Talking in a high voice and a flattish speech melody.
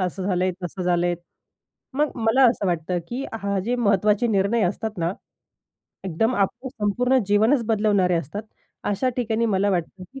No: high, 205 Hz; average, 4.1 semitones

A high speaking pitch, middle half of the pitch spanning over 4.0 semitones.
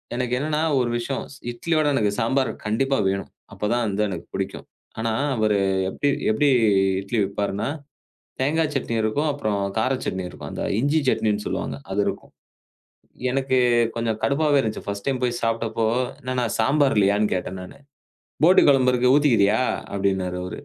No: low, 120 Hz; average, 4.6 semitones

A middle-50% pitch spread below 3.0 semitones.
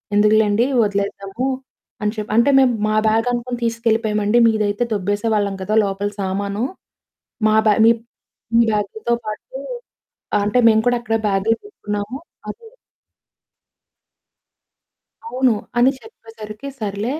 Yes: narrow, 2.5 semitones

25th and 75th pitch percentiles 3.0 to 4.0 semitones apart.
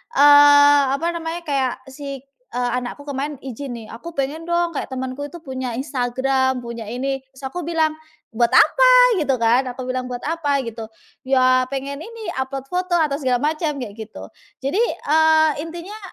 Yes: average, 3.7 semitones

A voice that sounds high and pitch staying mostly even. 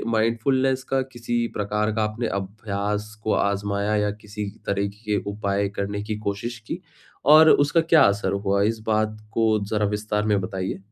No: low, 105 Hz; narrow, 2.2 semitones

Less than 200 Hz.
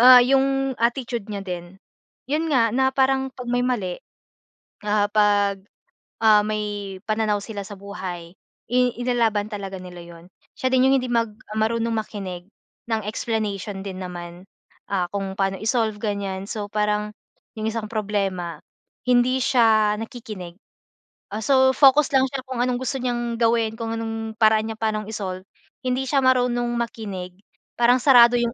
No: high, 220 Hz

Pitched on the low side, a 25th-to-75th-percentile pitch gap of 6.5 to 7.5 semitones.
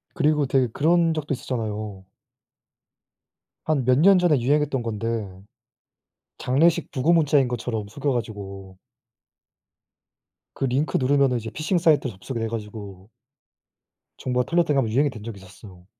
No: low, 125 Hz; wide, 5.4 semitones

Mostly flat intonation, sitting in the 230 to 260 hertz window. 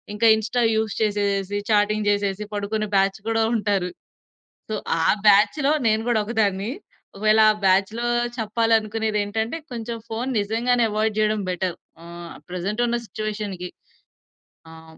No: narrow, 1.8 semitones; high, 215 Hz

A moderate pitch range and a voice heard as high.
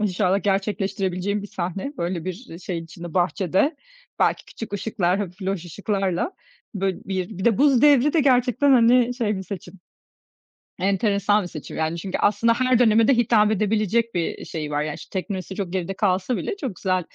Yes: average, 4.0 semitones; high, 195 Hz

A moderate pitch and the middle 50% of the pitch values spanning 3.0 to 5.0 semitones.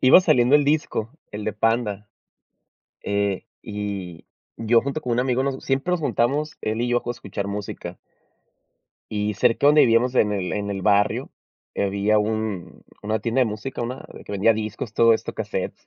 No: low, 110 Hz; average, 3.4 semitones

